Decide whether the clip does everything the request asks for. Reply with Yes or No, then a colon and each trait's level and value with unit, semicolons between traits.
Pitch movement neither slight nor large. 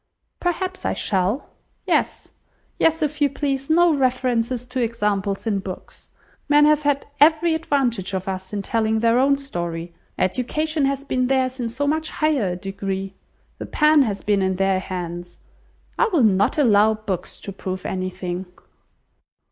No: wide, 6.9 semitones